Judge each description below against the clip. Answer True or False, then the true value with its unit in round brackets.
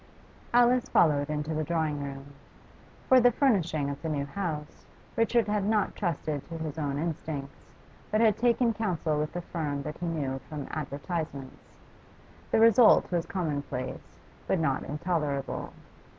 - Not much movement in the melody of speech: False (5.5 semitones)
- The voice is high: False (160 Hz)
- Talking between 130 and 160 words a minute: True (150 wpm)